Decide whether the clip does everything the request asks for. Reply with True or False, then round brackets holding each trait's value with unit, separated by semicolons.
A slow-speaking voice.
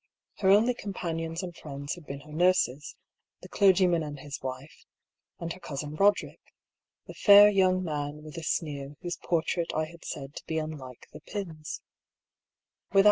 False (165 wpm)